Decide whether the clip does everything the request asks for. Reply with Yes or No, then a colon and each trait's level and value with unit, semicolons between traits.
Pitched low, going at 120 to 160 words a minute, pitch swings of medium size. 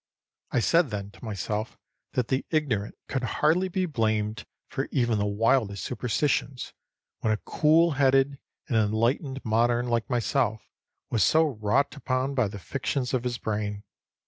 Yes: low, 120 Hz; average, 150 wpm; average, 4.2 semitones